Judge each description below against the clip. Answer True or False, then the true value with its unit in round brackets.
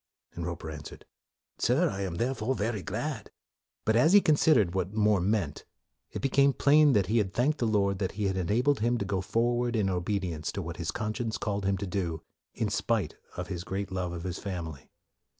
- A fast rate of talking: True (220 wpm)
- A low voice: True (100 Hz)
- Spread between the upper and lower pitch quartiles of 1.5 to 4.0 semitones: False (4.6 semitones)